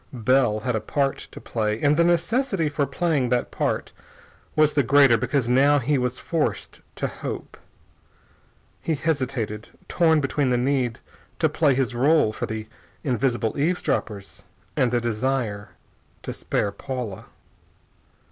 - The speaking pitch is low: Yes, low, 130 Hz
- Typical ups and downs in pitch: Yes, average, 3.9 semitones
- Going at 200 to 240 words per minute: No, average, 140 wpm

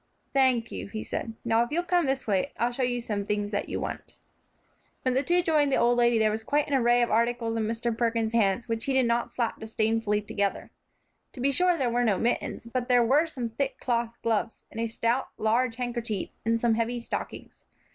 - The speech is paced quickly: Yes, fast, 225 wpm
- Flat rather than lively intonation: Yes, narrow, 2.2 semitones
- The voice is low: No, high, 235 Hz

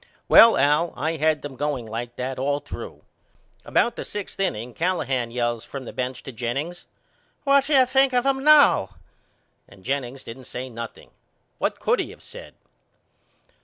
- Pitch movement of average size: No, wide, 7.6 semitones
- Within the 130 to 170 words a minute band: Yes, average, 165 wpm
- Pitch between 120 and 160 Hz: Yes, medium, 140 Hz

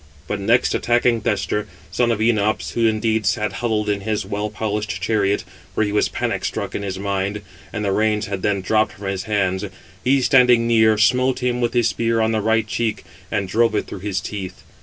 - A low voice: Yes, low, 105 Hz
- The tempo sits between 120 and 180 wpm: No, fast, 205 wpm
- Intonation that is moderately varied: No, narrow, 2.3 semitones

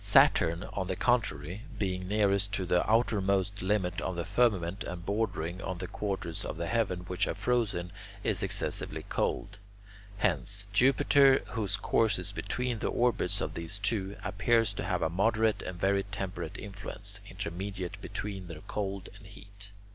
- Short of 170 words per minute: Yes, average, 160 wpm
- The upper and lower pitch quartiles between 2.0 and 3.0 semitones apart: Yes, narrow, 2.5 semitones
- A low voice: Yes, low, 100 Hz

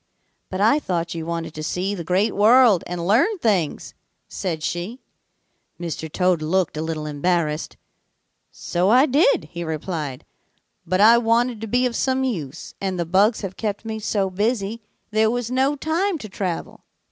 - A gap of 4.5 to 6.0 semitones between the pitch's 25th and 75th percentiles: Yes, wide, 5.6 semitones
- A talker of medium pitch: No, high, 195 Hz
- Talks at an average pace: Yes, average, 170 wpm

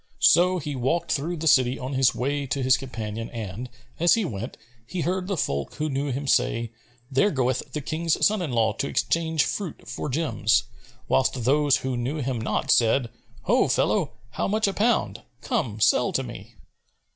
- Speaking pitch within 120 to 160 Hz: Yes, low, 135 Hz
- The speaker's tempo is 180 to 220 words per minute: Yes, average, 185 wpm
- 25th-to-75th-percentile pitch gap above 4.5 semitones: Yes, average, 5.2 semitones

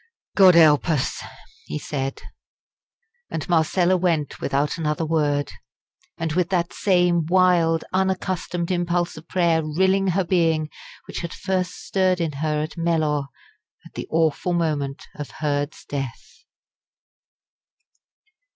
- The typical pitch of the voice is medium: Yes, medium, 165 Hz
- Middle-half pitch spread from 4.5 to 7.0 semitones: No, average, 2.9 semitones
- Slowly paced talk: Yes, slow, 125 wpm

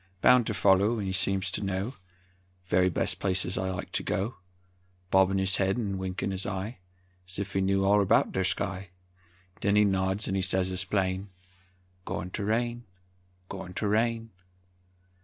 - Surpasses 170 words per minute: No, average, 165 wpm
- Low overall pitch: Yes, very low, 95 Hz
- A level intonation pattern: Yes, narrow, 1.6 semitones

